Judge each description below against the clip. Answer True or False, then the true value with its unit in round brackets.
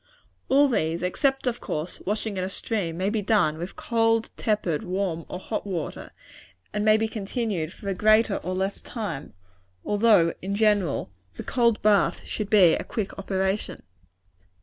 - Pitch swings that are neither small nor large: True (3.3 semitones)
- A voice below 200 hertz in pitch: False (205 Hz)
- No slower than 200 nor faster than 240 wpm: False (165 wpm)